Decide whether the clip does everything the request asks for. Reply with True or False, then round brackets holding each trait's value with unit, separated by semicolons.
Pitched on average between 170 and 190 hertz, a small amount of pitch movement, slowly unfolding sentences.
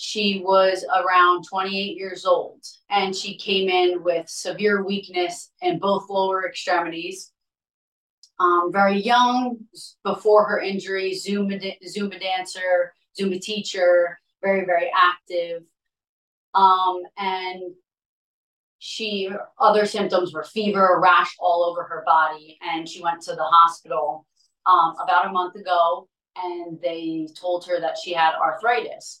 True (185 Hz; 2.3 semitones; 125 wpm)